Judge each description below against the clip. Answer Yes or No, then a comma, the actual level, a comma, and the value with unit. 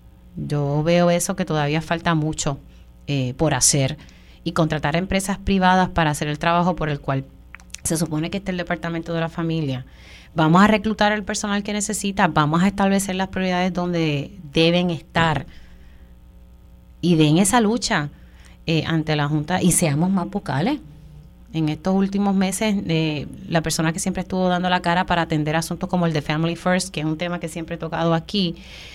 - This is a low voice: No, medium, 165 Hz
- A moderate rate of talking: Yes, average, 180 wpm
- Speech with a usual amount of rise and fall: Yes, average, 3.3 semitones